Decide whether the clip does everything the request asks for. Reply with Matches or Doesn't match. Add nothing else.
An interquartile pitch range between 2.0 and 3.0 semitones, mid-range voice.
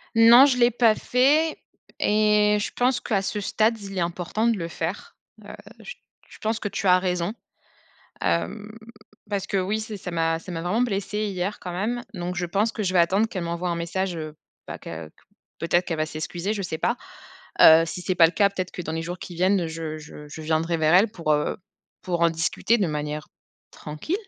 Doesn't match